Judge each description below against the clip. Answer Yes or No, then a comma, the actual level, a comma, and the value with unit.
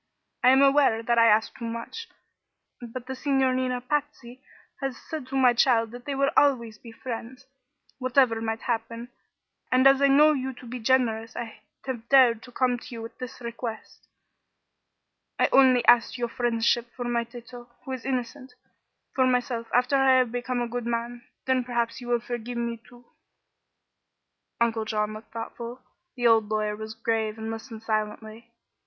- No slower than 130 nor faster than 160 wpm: No, average, 175 wpm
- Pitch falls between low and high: No, high, 240 Hz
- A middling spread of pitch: No, narrow, 2.1 semitones